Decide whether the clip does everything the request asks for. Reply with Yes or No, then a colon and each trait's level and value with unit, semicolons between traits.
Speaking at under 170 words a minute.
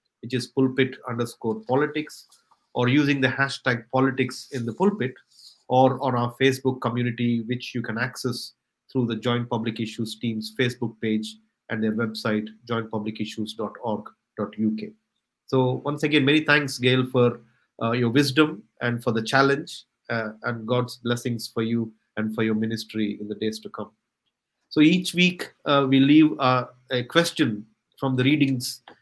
Yes: average, 155 wpm